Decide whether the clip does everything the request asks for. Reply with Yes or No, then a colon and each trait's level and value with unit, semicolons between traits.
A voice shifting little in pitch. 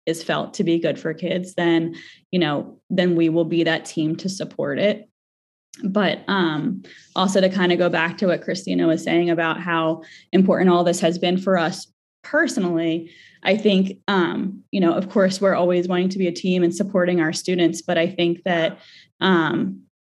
Yes: narrow, 2.2 semitones